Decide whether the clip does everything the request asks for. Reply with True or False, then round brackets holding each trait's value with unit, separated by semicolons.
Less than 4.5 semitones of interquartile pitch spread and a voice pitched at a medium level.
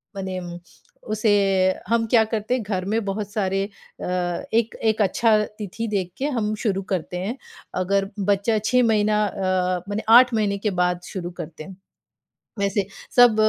False (2.6 semitones; 205 Hz)